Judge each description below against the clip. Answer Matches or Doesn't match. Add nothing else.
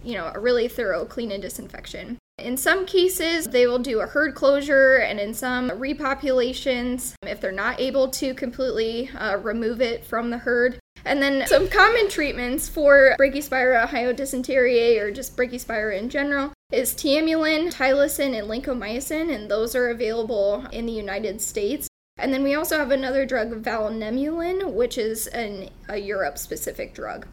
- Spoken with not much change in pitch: Doesn't match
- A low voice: Doesn't match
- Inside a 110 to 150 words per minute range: Doesn't match